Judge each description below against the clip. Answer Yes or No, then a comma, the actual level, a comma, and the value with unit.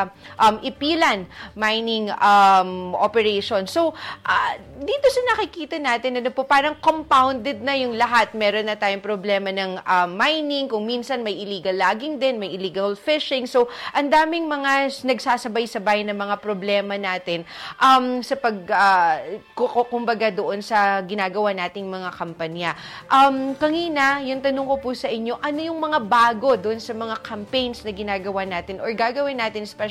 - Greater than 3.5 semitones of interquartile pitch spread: Yes, average, 5.3 semitones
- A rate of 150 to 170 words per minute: Yes, fast, 155 wpm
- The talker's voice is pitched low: No, high, 235 Hz